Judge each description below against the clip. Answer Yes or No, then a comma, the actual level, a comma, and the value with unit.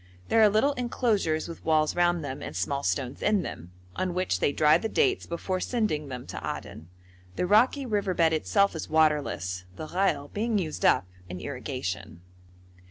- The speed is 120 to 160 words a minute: No, average, 175 wpm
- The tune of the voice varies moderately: No, wide, 6.6 semitones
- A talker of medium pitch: Yes, medium, 165 Hz